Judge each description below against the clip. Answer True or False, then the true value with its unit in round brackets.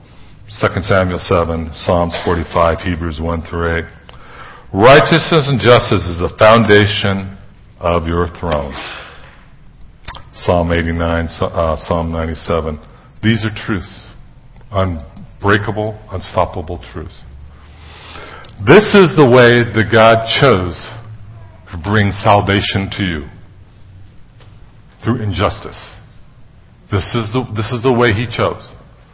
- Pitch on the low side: True (100 Hz)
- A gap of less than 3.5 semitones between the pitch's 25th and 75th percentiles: False (4.6 semitones)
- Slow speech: True (110 wpm)